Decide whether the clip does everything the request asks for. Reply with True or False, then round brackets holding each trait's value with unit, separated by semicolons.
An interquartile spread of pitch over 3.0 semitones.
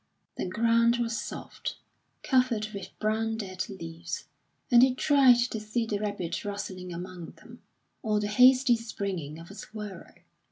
True (3.8 semitones)